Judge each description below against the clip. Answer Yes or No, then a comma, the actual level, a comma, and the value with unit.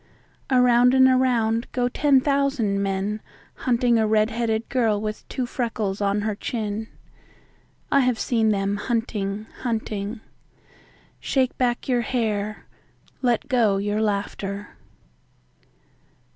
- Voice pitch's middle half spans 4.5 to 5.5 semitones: No, average, 3.1 semitones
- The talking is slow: Yes, slow, 110 wpm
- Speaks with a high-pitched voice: Yes, high, 225 Hz